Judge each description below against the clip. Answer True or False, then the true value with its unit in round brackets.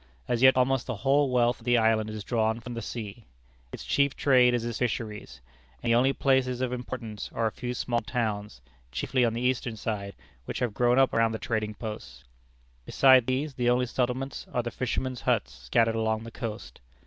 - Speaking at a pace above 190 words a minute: True (200 wpm)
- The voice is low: True (120 Hz)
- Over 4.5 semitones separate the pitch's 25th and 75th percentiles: False (2.4 semitones)